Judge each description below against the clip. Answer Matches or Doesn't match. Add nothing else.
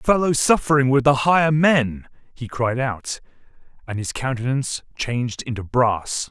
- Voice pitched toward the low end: Matches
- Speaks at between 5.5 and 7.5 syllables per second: Doesn't match